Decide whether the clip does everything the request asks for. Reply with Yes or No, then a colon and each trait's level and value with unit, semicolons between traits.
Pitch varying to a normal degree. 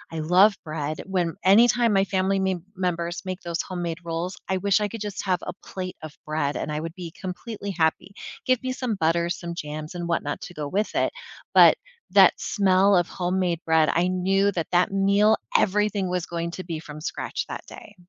Yes: average, 3.0 semitones